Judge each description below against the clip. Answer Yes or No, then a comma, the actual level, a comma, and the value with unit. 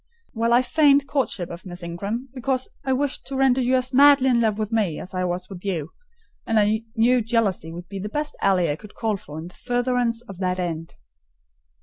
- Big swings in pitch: Yes, wide, 5.7 semitones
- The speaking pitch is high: Yes, high, 220 Hz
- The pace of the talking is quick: Yes, fast, 220 wpm